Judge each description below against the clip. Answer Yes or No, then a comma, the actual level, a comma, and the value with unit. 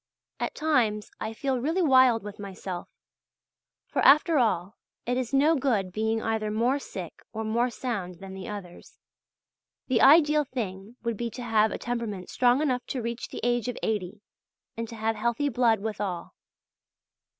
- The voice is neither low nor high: No, high, 230 Hz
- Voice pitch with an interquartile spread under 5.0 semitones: Yes, average, 3.4 semitones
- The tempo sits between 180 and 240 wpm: No, average, 165 wpm